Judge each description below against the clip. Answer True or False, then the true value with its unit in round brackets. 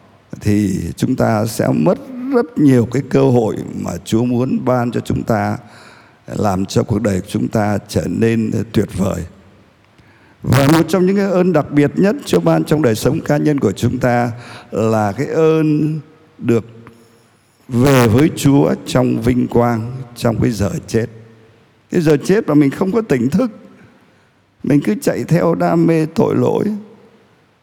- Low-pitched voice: True (125 Hz)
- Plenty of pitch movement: True (5.9 semitones)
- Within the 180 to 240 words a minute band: False (170 wpm)